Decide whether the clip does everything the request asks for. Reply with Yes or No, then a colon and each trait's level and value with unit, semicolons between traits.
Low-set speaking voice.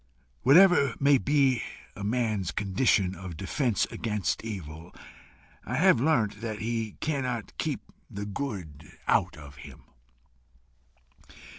Yes: low, 110 Hz